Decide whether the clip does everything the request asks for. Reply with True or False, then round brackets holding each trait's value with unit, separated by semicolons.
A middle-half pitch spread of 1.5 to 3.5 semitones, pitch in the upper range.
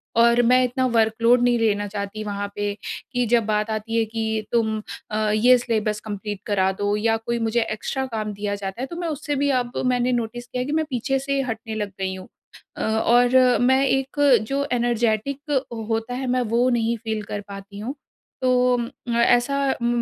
True (2.8 semitones; 235 Hz)